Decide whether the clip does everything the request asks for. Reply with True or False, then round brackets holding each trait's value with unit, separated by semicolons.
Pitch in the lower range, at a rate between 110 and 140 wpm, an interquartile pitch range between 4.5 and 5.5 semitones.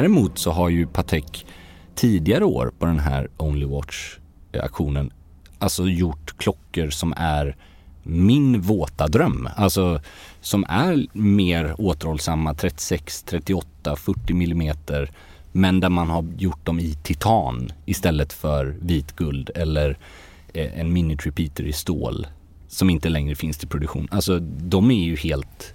False (80 Hz; 135 wpm; 3.2 semitones)